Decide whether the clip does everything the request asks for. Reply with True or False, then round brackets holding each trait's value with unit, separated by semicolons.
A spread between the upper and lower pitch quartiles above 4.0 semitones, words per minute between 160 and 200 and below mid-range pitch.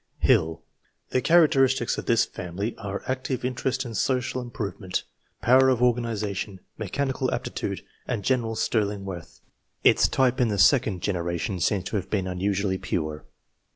False (4.8 semitones; 145 wpm; 110 Hz)